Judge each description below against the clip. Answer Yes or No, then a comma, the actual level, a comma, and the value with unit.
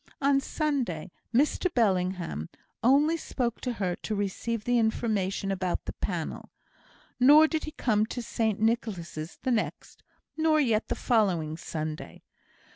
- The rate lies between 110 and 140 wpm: Yes, slow, 135 wpm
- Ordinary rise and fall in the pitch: No, wide, 5.7 semitones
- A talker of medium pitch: No, high, 225 Hz